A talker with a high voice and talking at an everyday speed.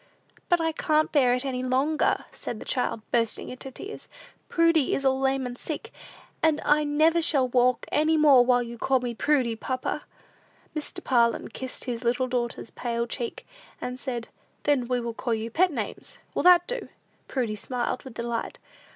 Yes: very high, 255 Hz; average, 175 wpm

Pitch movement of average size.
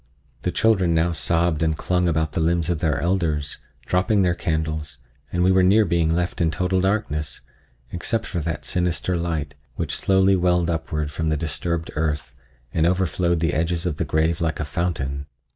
No: narrow, 2.3 semitones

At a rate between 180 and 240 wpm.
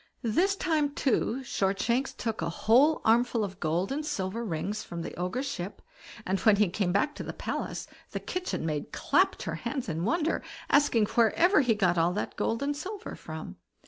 Yes: average, 185 wpm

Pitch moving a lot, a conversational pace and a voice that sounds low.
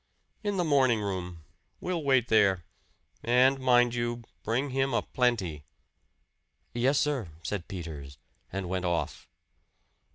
No: wide, 6.5 semitones; slow, 125 wpm; low, 120 Hz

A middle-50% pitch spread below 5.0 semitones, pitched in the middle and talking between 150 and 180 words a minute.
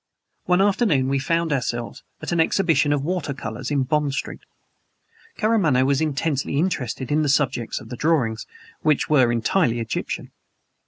Yes: average, 4.1 semitones; medium, 145 Hz; average, 155 wpm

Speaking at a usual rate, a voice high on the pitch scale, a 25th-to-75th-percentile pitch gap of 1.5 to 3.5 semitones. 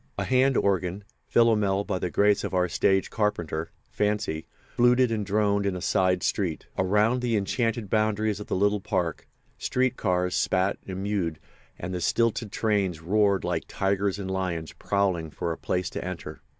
No: average, 165 wpm; low, 100 Hz; average, 2.7 semitones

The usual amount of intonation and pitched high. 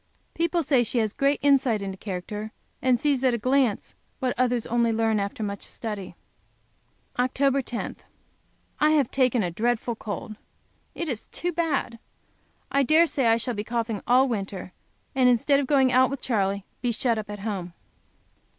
Yes: average, 3.9 semitones; high, 240 Hz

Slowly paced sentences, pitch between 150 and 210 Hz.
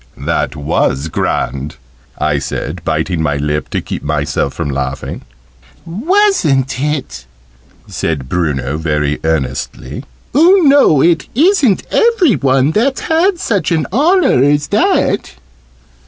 No: slow, 120 wpm; low, 130 Hz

